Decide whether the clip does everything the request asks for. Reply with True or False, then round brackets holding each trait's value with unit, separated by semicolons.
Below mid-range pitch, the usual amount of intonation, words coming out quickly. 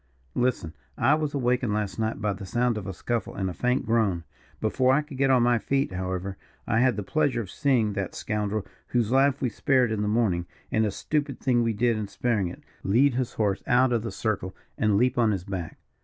True (115 Hz; 3.9 semitones; 225 wpm)